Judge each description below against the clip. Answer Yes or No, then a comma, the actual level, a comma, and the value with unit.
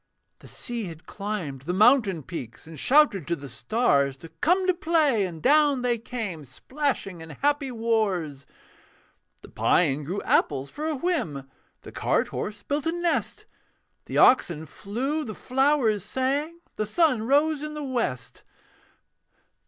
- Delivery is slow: No, average, 150 wpm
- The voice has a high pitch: Yes, high, 225 Hz